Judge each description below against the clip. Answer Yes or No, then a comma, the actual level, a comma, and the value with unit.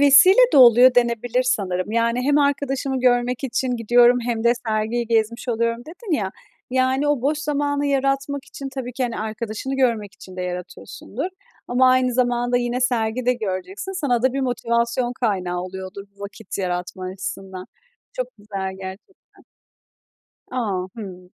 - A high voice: Yes, high, 240 Hz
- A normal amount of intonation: Yes, average, 3.8 semitones